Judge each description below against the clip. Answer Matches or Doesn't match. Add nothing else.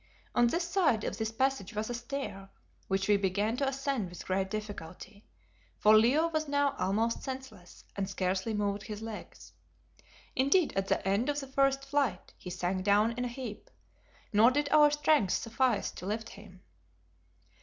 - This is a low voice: Doesn't match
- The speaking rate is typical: Matches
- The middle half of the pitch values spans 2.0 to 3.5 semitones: Doesn't match